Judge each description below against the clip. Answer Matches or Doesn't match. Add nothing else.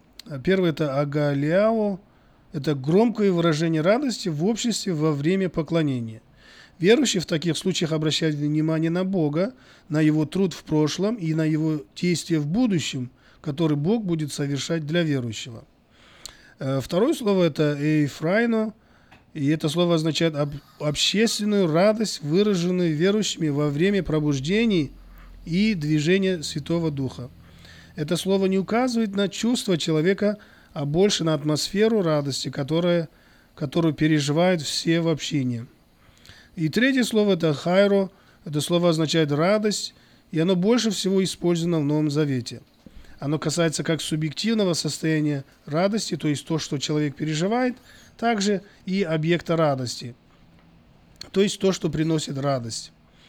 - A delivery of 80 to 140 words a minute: Matches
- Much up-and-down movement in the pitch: Doesn't match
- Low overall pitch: Doesn't match